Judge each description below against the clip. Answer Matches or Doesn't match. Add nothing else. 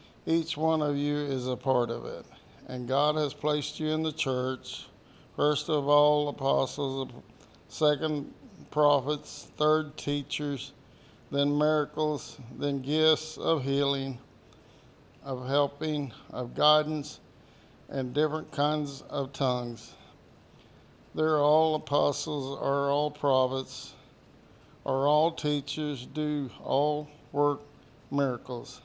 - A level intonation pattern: Matches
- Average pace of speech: Doesn't match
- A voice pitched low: Doesn't match